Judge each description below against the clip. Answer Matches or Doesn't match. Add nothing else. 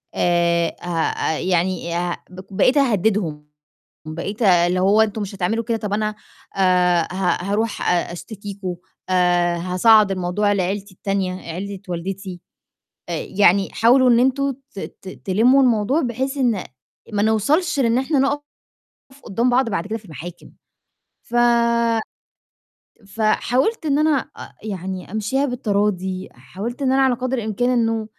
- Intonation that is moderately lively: Matches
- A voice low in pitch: Doesn't match